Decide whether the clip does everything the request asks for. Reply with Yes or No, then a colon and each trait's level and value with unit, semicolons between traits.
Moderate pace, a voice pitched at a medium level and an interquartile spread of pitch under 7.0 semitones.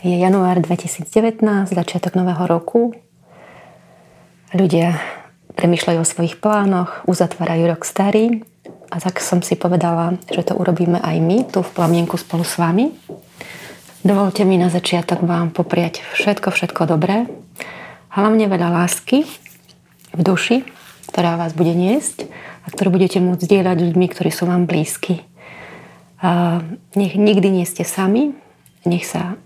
Yes: average, 130 wpm; medium, 180 Hz; narrow, 2.5 semitones